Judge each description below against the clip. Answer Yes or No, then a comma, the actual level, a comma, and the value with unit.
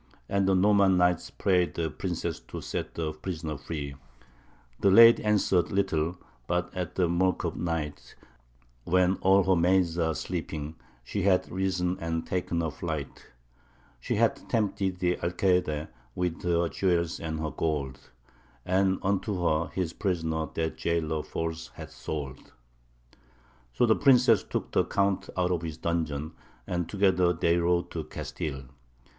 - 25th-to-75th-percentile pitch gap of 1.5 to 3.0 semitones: Yes, average, 2.7 semitones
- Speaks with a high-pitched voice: No, very low, 85 Hz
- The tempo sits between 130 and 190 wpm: Yes, average, 150 wpm